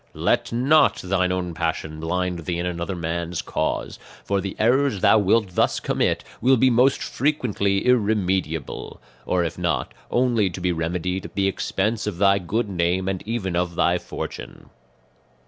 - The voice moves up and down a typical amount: Yes, average, 4.0 semitones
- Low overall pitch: Yes, very low, 95 Hz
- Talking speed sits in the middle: Yes, average, 165 wpm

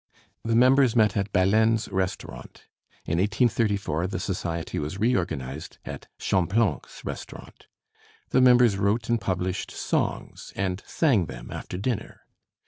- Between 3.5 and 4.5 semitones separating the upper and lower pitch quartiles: Yes, average, 4.0 semitones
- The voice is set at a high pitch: No, low, 100 Hz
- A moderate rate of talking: No, slow, 125 wpm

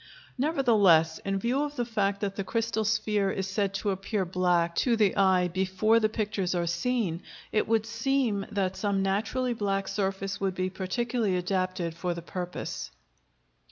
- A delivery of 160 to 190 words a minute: Yes, average, 165 wpm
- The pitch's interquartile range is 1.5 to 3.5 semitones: Yes, average, 3.2 semitones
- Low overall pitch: No, high, 195 Hz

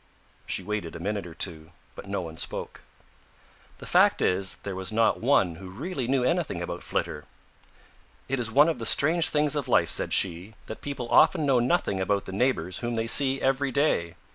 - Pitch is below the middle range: Yes, low, 115 Hz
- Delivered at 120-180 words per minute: No, average, 195 wpm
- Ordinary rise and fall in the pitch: No, wide, 6.5 semitones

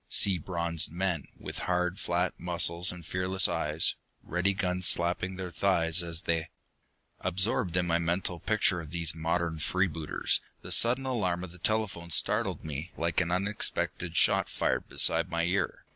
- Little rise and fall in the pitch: Yes, narrow, 1.9 semitones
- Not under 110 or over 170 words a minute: Yes, average, 160 wpm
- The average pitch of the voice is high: No, very low, 90 Hz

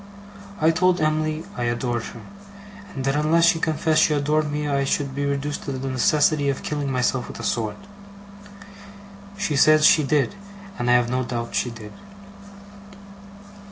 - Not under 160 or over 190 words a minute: Yes, average, 165 wpm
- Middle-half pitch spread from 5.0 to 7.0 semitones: No, average, 3.2 semitones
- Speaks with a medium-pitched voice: Yes, medium, 145 Hz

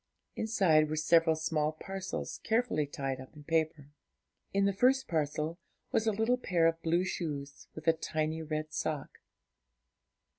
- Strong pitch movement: No, average, 3.8 semitones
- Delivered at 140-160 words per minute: Yes, average, 150 wpm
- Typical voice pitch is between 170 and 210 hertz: No, medium, 160 Hz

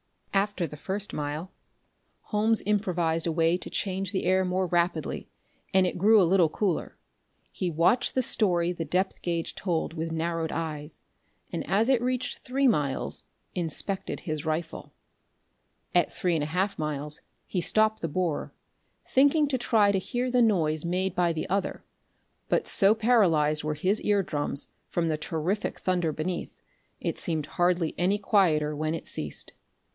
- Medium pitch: Yes, medium, 180 Hz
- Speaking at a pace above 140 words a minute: Yes, average, 160 wpm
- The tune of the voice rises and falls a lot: No, average, 3.9 semitones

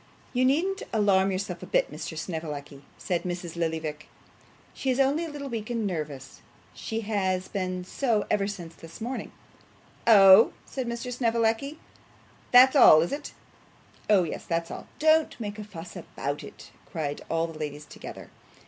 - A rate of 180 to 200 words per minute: No, average, 160 wpm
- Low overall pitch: No, high, 200 Hz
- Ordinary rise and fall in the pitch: No, wide, 6.8 semitones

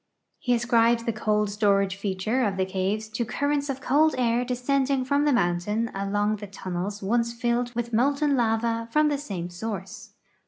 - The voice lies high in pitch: Yes, high, 230 Hz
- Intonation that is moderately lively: Yes, average, 3.9 semitones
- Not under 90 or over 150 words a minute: No, average, 170 wpm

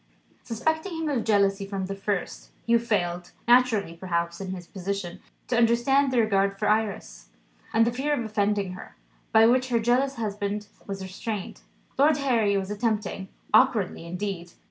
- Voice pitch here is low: No, high, 210 Hz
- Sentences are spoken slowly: No, average, 160 wpm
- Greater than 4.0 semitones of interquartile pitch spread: No, average, 3.5 semitones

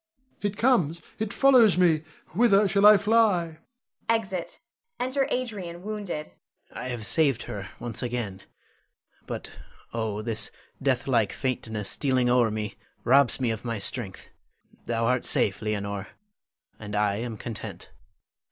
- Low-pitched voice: Yes, low, 130 Hz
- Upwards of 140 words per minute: No, slow, 135 wpm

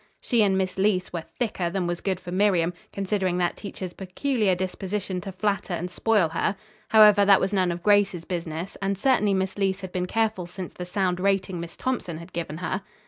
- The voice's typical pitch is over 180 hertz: Yes, high, 190 Hz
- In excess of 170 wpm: Yes, average, 200 wpm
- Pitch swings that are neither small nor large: No, narrow, 2.3 semitones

